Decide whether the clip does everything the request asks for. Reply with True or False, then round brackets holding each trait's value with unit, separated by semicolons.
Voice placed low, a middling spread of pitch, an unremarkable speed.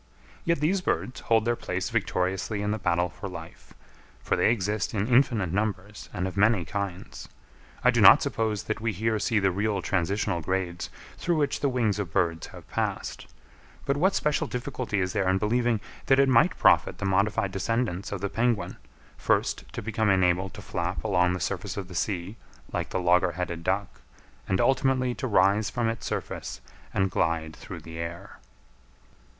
True (100 Hz; 3.9 semitones; 180 wpm)